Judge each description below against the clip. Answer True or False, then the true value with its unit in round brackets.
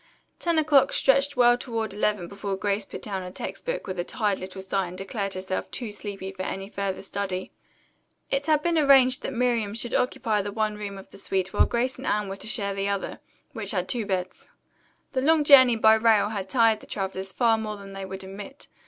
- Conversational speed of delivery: False (215 wpm)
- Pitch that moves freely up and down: False (3.9 semitones)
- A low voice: False (210 Hz)